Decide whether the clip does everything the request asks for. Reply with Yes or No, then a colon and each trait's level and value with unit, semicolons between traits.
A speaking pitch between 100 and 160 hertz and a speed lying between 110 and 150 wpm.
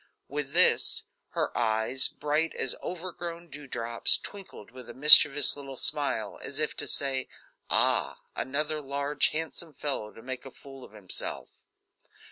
Yes: medium, 140 Hz; average, 145 wpm